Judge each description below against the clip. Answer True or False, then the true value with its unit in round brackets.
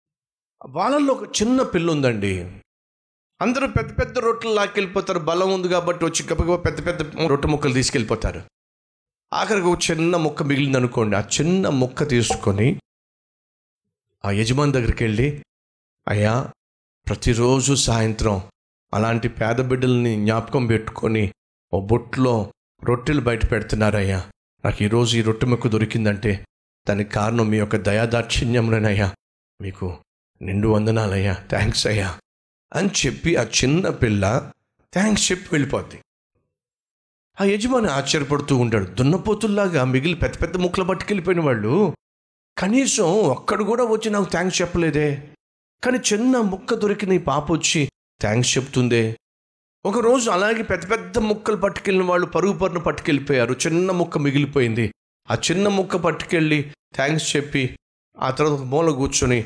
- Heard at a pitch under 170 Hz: True (140 Hz)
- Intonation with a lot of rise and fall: True (8.3 semitones)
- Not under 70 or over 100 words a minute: False (115 wpm)